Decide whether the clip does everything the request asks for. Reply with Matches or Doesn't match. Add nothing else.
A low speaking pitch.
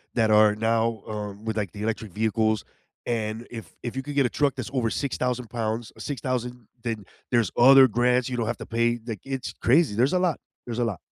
Matches